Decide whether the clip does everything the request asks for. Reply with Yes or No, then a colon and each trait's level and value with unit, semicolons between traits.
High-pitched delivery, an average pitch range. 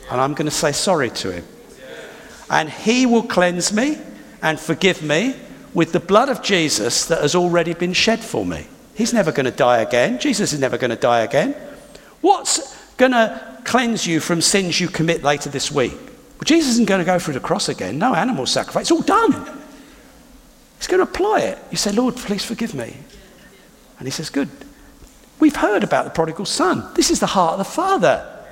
No: high, 220 Hz; wide, 8.1 semitones